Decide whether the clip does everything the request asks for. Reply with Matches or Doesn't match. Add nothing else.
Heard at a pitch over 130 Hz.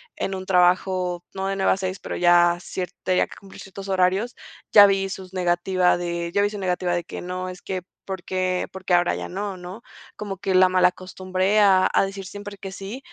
Matches